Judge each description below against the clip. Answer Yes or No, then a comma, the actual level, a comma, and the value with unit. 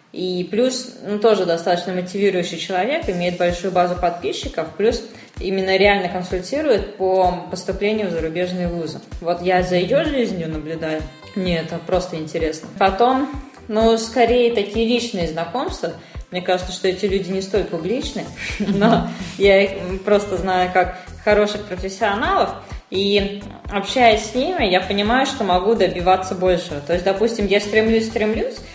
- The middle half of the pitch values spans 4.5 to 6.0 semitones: No, average, 3.2 semitones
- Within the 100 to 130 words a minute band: No, average, 140 wpm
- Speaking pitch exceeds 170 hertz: Yes, high, 190 Hz